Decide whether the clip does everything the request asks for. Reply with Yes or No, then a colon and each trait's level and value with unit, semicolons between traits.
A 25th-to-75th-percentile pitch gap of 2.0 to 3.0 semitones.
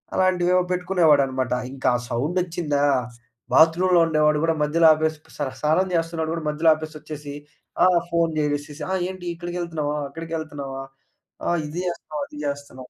Yes: average, 2.7 semitones